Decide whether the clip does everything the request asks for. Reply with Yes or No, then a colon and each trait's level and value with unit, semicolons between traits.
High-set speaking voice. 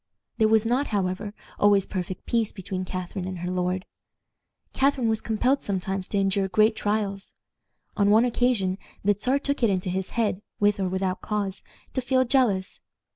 Yes: high, 205 Hz